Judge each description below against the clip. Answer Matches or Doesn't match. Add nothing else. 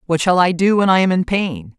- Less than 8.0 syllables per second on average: Matches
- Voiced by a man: Doesn't match